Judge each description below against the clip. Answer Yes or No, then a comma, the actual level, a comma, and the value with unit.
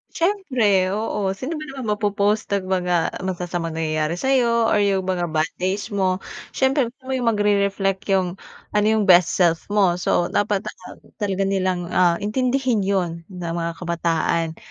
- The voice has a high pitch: Yes, high, 195 Hz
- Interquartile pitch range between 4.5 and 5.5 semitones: No, average, 3.6 semitones